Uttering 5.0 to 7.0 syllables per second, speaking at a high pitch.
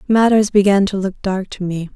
Yes: 5.4 syllables/s; high, 195 Hz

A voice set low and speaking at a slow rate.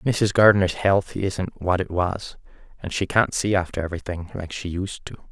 No: very low, 95 Hz; fast, 205 wpm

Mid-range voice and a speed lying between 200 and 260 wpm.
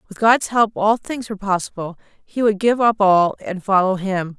No: high, 205 Hz; fast, 205 wpm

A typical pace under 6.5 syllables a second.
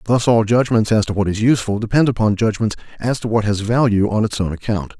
No: 6.6 syllables/s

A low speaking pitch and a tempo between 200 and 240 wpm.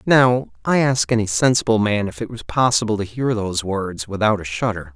Yes: low, 110 Hz; fast, 205 wpm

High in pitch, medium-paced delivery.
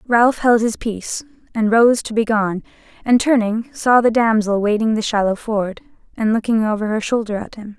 Yes: high, 220 Hz; average, 195 wpm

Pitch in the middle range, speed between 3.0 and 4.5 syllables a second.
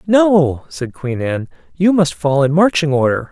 Yes: medium, 155 Hz; 4.2 syllables/s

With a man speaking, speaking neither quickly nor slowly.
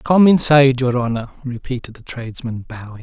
Yes: male; average, 160 wpm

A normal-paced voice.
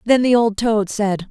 No: fast, 230 wpm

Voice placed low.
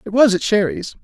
No: high, 190 Hz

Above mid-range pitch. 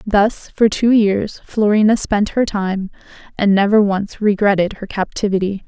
Yes: high, 205 Hz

